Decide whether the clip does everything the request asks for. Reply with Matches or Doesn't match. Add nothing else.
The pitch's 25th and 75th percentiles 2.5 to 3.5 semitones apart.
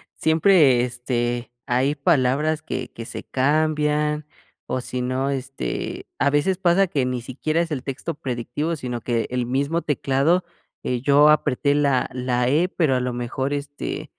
Matches